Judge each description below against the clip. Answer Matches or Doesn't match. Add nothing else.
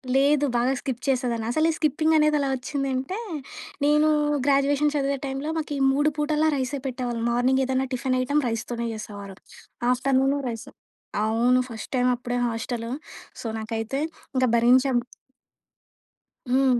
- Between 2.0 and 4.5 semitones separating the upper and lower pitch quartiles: Matches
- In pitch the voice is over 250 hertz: Matches